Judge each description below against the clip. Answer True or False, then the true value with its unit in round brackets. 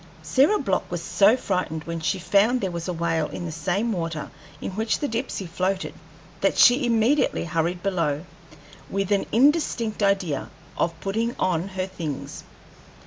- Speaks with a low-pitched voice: False (190 Hz)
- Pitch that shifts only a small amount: False (4.8 semitones)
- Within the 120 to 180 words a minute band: True (160 wpm)